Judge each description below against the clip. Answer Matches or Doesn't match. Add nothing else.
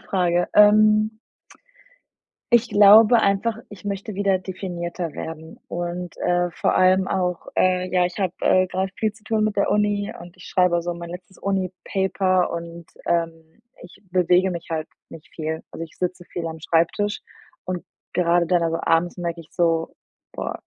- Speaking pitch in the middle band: Matches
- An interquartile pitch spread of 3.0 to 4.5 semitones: Doesn't match